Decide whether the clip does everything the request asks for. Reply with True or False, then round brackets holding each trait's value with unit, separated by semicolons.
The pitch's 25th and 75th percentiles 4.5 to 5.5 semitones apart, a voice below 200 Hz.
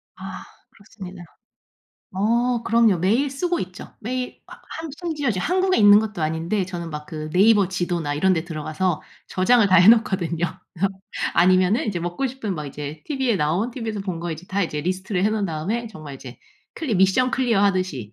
True (5.2 semitones; 190 Hz)